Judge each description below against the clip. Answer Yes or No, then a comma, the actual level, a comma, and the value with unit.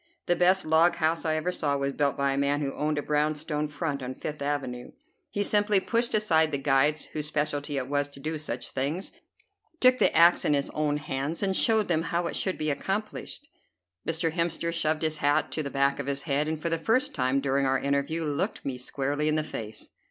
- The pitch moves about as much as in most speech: Yes, average, 3.0 semitones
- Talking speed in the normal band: No, fast, 225 wpm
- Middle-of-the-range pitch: Yes, medium, 150 Hz